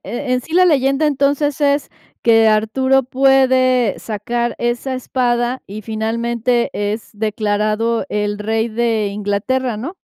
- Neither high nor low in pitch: No, high, 235 Hz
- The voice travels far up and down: No, average, 3.3 semitones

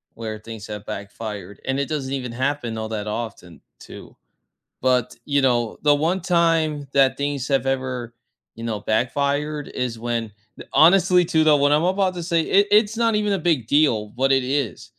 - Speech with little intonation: No, wide, 5.4 semitones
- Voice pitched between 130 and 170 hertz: Yes, low, 135 Hz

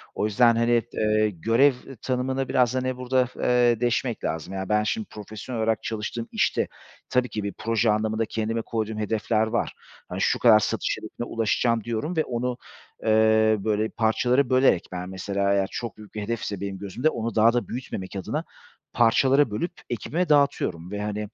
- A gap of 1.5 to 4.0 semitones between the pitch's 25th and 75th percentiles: Yes, narrow, 2.6 semitones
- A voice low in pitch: Yes, low, 115 Hz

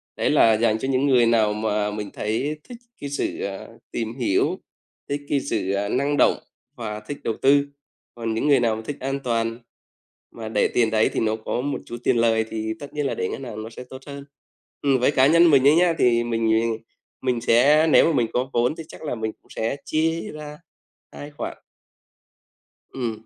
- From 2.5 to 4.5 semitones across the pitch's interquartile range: Yes, average, 4.2 semitones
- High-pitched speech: No, low, 120 Hz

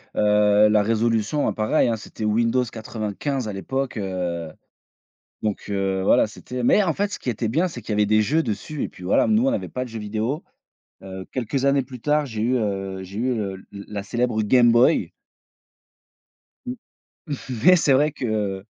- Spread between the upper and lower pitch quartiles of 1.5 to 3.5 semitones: No, average, 4.0 semitones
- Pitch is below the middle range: Yes, low, 110 Hz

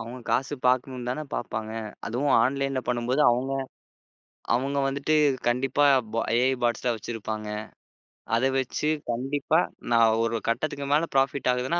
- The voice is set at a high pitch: No, low, 125 Hz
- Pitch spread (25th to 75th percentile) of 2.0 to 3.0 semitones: Yes, narrow, 2.6 semitones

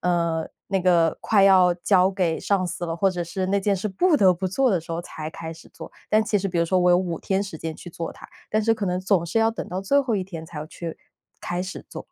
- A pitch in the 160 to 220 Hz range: Yes, medium, 185 Hz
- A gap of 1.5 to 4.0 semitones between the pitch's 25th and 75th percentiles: Yes, average, 2.8 semitones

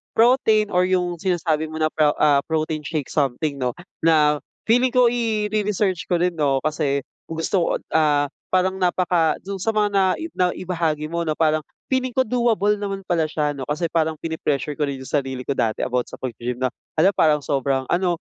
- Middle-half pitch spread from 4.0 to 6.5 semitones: Yes, average, 4.5 semitones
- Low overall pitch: No, medium, 160 Hz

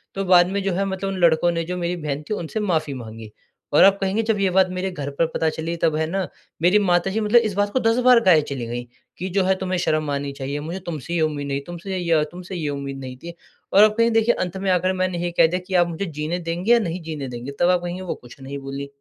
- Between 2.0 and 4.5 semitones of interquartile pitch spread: Yes, average, 4.0 semitones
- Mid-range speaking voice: Yes, medium, 175 Hz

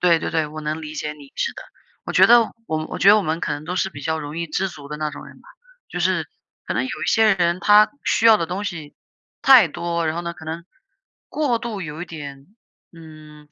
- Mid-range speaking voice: Yes, medium, 165 Hz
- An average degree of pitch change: Yes, average, 4.2 semitones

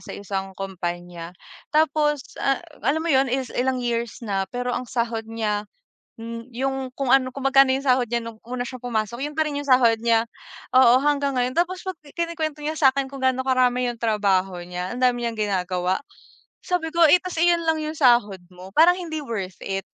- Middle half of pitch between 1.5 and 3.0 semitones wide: No, average, 4.2 semitones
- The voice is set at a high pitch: Yes, very high, 250 Hz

